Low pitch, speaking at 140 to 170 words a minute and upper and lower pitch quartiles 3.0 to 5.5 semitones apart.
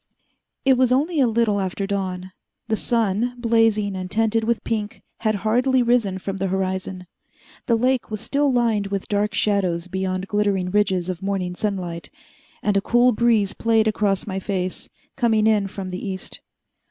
No: high, 205 Hz; average, 165 wpm; average, 3.3 semitones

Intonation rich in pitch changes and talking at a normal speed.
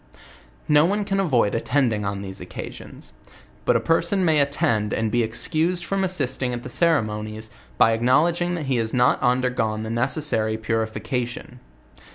Yes: wide, 6.2 semitones; average, 170 wpm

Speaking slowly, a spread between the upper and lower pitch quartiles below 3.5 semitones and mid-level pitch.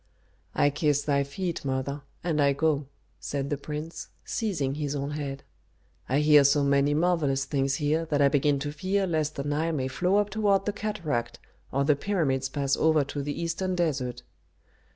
No: average, 180 wpm; average, 2.9 semitones; medium, 145 Hz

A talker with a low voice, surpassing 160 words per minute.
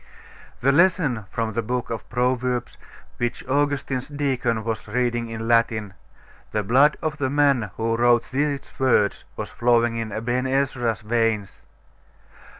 No: low, 120 Hz; average, 140 wpm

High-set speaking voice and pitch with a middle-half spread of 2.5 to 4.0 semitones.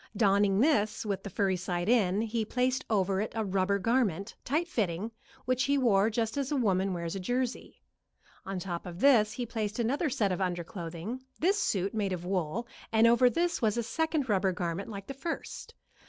No: high, 210 Hz; average, 4.6 semitones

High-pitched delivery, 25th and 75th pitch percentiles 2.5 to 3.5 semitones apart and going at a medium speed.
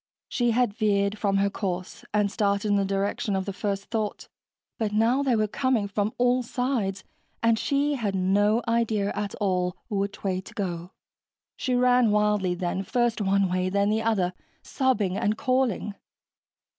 Yes: high, 205 Hz; average, 2.8 semitones; average, 170 wpm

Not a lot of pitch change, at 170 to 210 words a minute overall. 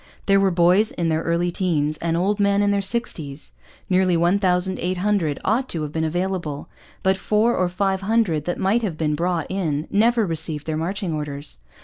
No: average, 3.7 semitones; average, 185 wpm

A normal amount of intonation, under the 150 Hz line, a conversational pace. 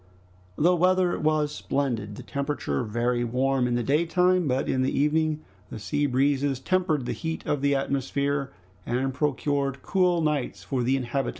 Yes: average, 3.1 semitones; medium, 140 Hz; average, 185 wpm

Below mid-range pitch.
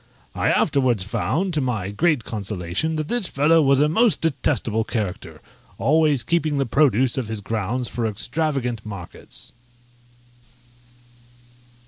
Yes: low, 130 Hz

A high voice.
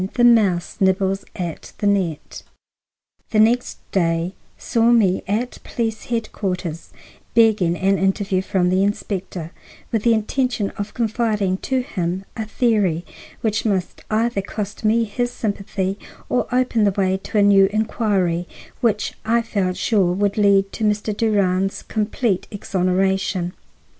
Yes: high, 200 Hz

